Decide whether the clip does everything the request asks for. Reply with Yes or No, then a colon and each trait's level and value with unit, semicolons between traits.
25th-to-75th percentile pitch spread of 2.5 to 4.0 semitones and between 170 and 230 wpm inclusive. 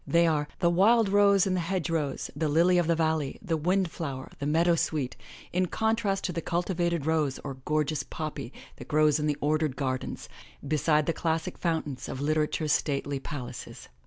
Yes: average, 2.9 semitones; average, 180 wpm